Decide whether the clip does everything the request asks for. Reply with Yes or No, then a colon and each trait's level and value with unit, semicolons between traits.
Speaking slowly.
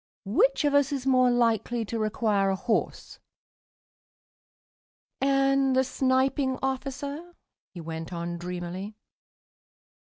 Yes: slow, 110 wpm